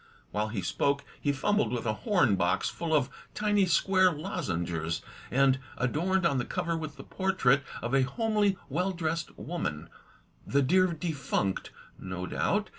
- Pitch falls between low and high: Yes, medium, 145 Hz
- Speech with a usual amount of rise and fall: No, wide, 7.3 semitones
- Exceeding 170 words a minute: No, average, 155 wpm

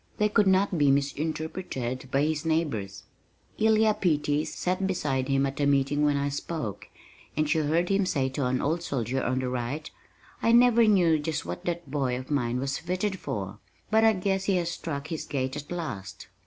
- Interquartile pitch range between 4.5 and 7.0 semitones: Yes, average, 5.1 semitones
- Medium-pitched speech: Yes, medium, 150 Hz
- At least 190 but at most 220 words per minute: Yes, average, 195 wpm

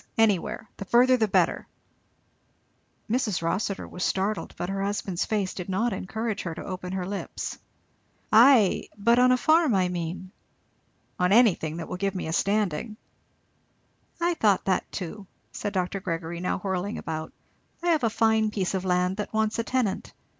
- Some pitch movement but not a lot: Yes, average, 3.4 semitones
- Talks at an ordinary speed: Yes, average, 165 wpm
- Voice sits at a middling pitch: No, high, 200 Hz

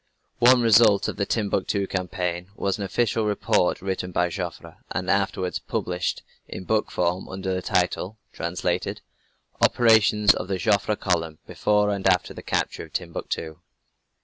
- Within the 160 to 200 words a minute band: No, average, 150 wpm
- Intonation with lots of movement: No, narrow, 2.6 semitones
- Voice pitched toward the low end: Yes, very low, 95 Hz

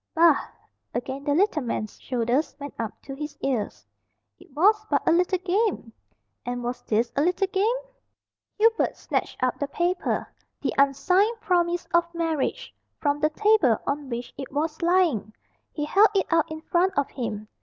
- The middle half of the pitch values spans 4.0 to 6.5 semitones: Yes, wide, 5.5 semitones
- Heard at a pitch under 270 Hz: No, very high, 305 Hz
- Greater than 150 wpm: Yes, average, 165 wpm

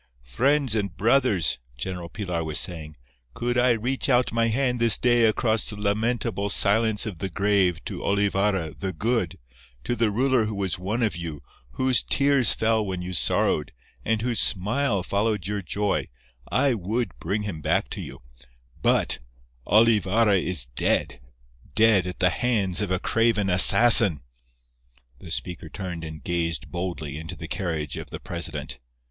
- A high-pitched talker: No, low, 100 Hz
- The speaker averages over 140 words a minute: Yes, average, 155 wpm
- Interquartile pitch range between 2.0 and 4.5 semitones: No, average, 5.1 semitones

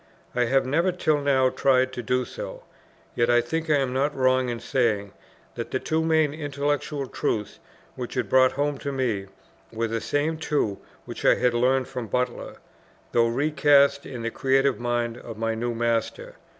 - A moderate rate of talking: Yes, average, 180 wpm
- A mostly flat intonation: No, average, 3.4 semitones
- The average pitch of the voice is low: Yes, low, 130 Hz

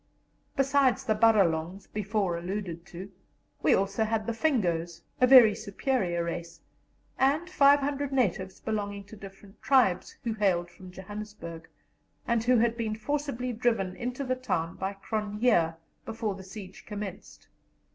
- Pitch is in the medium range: No, high, 210 Hz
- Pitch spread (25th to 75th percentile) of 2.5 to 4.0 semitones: No, average, 4.5 semitones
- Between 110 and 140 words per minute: Yes, slow, 135 wpm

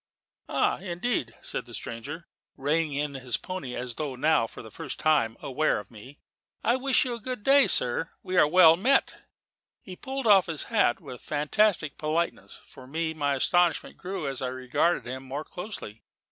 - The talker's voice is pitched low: No, medium, 155 Hz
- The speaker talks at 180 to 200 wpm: Yes, average, 190 wpm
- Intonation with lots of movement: Yes, wide, 6.1 semitones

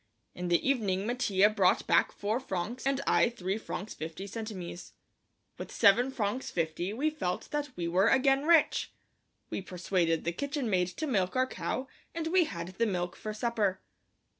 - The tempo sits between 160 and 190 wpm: Yes, average, 170 wpm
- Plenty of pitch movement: Yes, wide, 6.1 semitones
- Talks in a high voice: Yes, high, 210 Hz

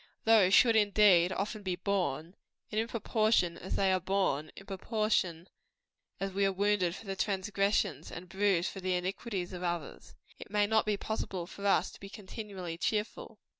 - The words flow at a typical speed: Yes, average, 175 wpm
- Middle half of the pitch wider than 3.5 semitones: No, narrow, 2.5 semitones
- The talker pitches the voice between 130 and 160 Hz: No, high, 195 Hz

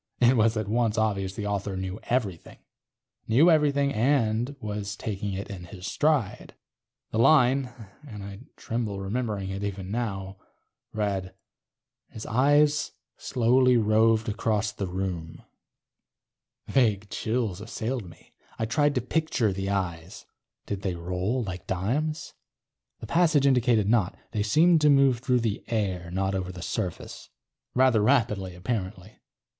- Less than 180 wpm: Yes, average, 140 wpm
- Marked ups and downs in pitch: No, average, 4.5 semitones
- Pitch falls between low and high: No, low, 110 Hz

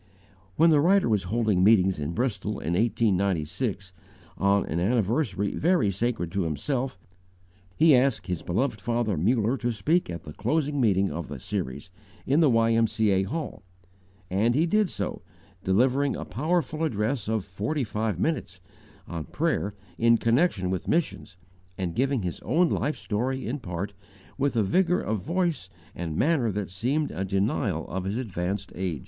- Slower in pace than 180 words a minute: Yes, average, 160 wpm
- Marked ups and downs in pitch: Yes, wide, 6.3 semitones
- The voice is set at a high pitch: No, low, 110 Hz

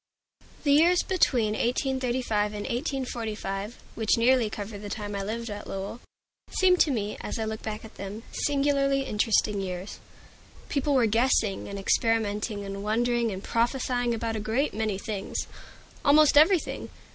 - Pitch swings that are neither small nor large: Yes, average, 3.9 semitones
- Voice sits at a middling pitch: No, high, 225 Hz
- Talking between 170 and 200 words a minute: No, average, 155 wpm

